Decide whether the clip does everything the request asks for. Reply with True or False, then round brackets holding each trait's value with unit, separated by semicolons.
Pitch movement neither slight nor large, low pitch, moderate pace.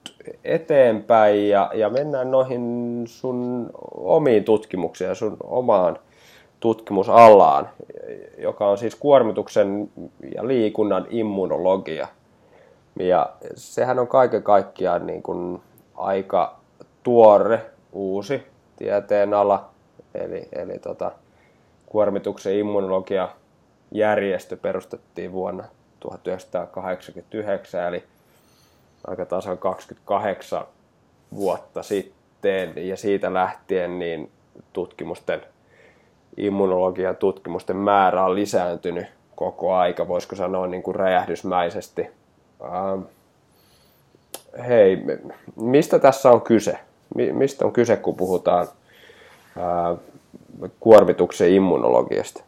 False (4.8 semitones; 105 Hz; 85 wpm)